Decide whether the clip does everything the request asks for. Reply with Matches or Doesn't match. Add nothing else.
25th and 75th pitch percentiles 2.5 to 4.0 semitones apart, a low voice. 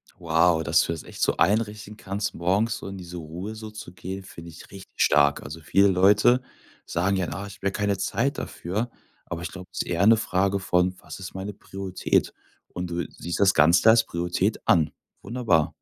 Matches